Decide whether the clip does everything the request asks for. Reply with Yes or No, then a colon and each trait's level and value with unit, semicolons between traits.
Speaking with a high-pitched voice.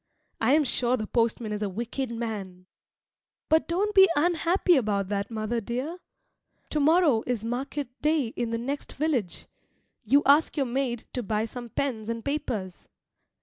Yes: high, 240 Hz